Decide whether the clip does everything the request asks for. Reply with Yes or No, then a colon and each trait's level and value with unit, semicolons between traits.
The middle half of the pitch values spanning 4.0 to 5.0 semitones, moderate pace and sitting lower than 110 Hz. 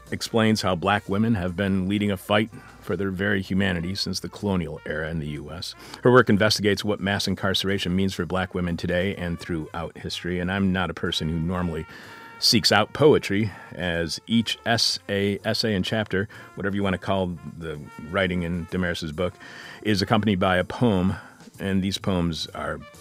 No: narrow, 2.6 semitones; average, 180 wpm; very low, 95 Hz